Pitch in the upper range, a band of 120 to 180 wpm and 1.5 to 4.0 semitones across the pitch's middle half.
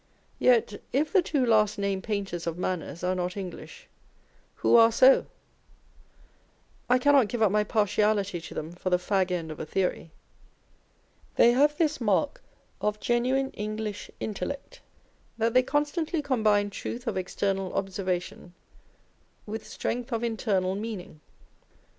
No: high, 210 Hz; average, 140 wpm; average, 4.7 semitones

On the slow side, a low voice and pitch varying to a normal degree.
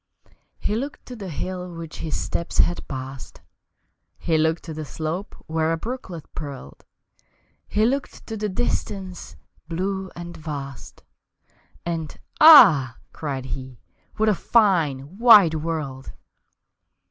No: slow, 125 wpm; medium, 165 Hz; average, 4.8 semitones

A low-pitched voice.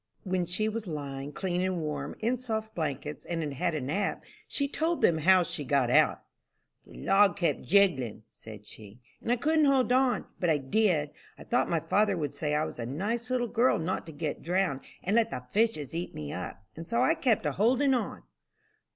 No: medium, 180 Hz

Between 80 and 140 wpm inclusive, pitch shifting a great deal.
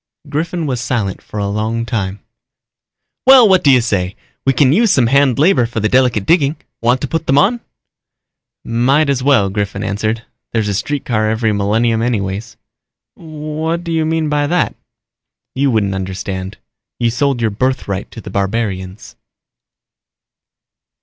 No: average, 155 wpm; wide, 5.8 semitones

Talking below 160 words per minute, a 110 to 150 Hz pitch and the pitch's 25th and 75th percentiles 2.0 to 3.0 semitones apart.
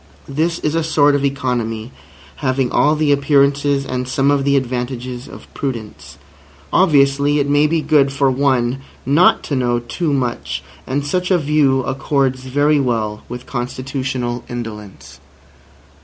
Yes: average, 145 wpm; low, 135 Hz; narrow, 2.6 semitones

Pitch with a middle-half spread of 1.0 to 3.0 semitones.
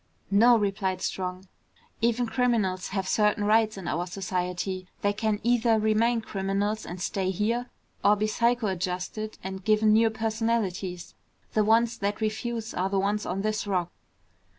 Yes: average, 2.7 semitones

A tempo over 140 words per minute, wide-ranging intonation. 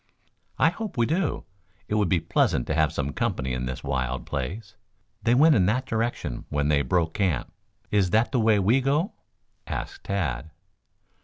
Yes: average, 175 wpm; wide, 9.0 semitones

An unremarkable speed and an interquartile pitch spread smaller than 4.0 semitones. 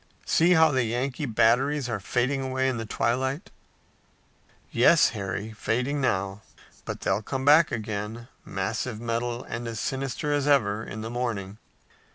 Yes: average, 150 wpm; average, 3.6 semitones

